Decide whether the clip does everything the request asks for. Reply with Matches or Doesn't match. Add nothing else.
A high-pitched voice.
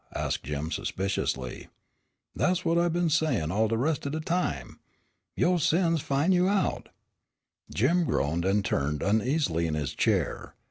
Doesn't match